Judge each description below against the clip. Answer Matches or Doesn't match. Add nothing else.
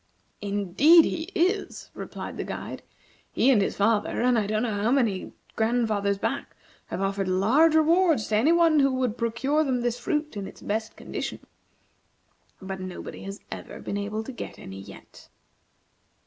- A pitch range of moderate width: Doesn't match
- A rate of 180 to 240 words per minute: Doesn't match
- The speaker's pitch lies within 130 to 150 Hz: Doesn't match